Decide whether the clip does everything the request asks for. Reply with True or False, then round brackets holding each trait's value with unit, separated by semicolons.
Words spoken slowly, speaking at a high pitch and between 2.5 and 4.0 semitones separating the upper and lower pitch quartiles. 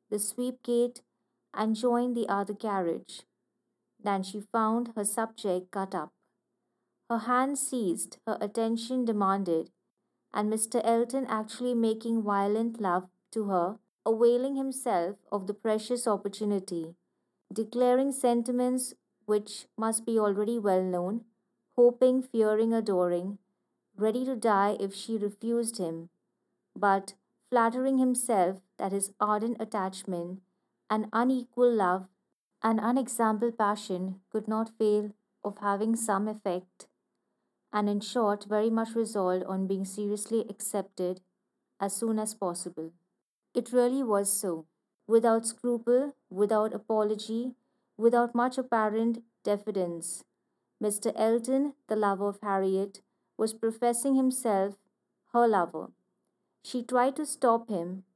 True (120 wpm; 215 Hz; 3.2 semitones)